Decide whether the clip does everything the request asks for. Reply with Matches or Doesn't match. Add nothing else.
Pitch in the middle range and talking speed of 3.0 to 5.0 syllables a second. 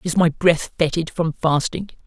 Matches